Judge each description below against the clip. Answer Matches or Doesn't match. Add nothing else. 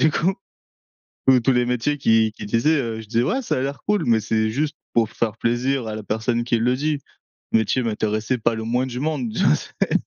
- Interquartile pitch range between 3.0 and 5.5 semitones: Matches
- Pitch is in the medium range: Doesn't match